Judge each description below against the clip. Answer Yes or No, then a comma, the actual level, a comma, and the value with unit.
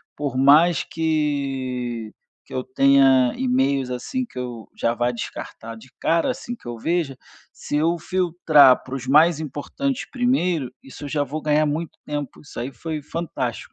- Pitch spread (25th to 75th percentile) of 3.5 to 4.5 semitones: Yes, average, 4.1 semitones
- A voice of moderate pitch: Yes, medium, 145 Hz